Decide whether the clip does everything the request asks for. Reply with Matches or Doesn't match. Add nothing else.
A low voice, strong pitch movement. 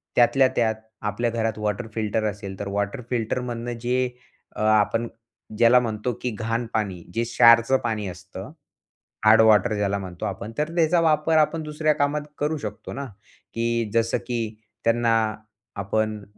Doesn't match